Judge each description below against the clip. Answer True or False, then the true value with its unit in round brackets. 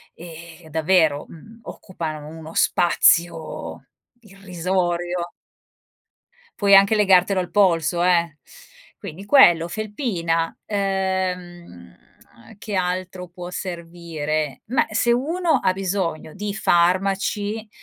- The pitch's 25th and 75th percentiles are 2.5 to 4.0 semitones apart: True (2.9 semitones)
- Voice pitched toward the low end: False (180 Hz)